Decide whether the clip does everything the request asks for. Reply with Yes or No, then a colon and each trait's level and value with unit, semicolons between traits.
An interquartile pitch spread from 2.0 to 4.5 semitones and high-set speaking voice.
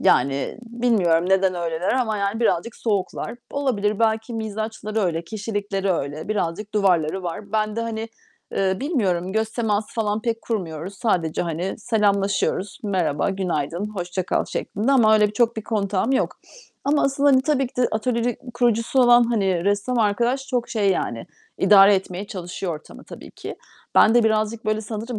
Yes: average, 3.4 semitones; high, 210 Hz